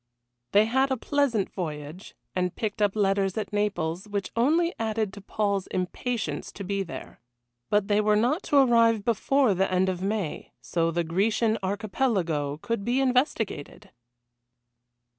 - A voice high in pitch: Yes, high, 205 Hz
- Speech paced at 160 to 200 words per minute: No, average, 150 wpm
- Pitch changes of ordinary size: Yes, average, 3.7 semitones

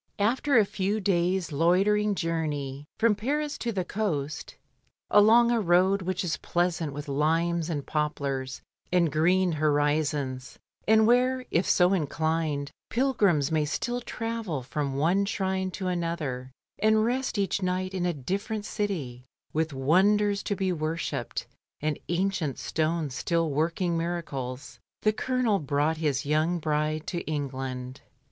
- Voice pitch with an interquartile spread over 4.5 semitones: Yes, average, 5.1 semitones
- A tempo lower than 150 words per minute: Yes, average, 140 wpm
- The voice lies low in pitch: No, medium, 170 Hz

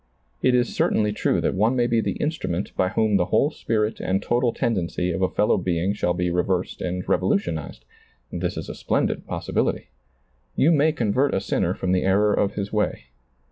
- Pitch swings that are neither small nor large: Yes, average, 4.4 semitones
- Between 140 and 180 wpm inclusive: No, average, 190 wpm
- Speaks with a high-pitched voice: No, low, 105 Hz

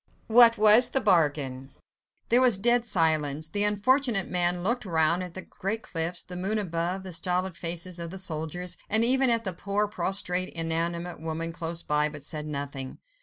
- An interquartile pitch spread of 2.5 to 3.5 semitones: No, average, 4.2 semitones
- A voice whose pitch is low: No, medium, 180 Hz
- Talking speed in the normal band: Yes, average, 175 wpm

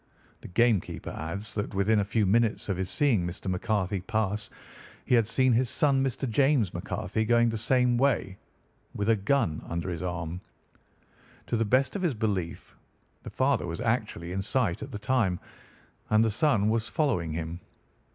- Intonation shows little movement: No, average, 4.4 semitones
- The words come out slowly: No, average, 180 wpm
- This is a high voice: No, low, 110 Hz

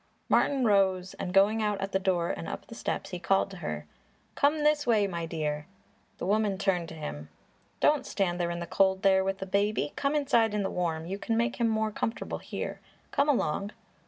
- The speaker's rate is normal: No, fast, 210 wpm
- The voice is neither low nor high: No, high, 195 Hz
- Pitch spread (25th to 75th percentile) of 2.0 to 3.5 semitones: No, average, 3.9 semitones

